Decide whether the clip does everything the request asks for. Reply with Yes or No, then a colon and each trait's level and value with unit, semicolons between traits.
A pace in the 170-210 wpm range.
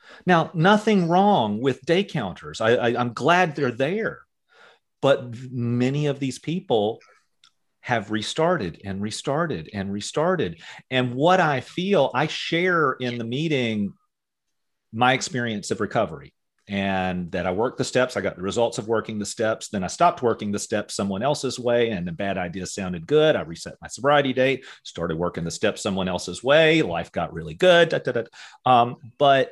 Yes: average, 175 wpm